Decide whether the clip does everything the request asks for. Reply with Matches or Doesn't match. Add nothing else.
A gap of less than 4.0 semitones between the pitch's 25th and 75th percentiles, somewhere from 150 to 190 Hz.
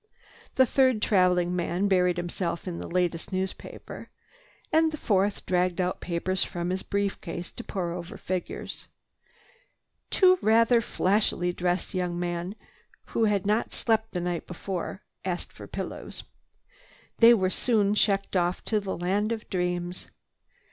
Matches